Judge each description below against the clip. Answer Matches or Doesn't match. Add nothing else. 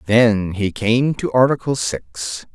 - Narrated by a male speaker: Matches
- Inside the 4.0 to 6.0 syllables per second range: Doesn't match